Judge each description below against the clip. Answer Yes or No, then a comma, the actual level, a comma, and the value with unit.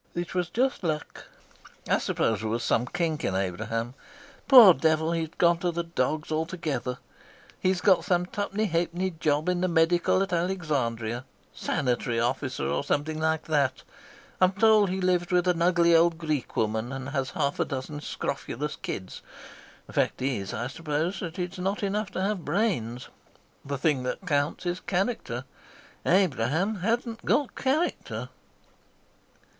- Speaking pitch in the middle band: Yes, medium, 165 Hz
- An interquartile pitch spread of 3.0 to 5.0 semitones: No, wide, 5.5 semitones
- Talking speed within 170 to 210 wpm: No, average, 155 wpm